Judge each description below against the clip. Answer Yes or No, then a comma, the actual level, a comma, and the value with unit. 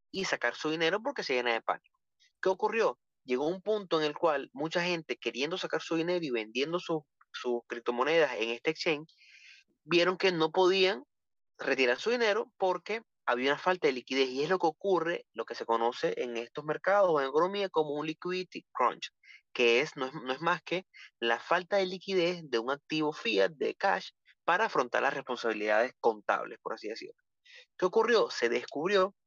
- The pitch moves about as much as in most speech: No, wide, 5.8 semitones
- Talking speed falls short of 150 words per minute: No, fast, 190 wpm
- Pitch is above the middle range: No, medium, 165 Hz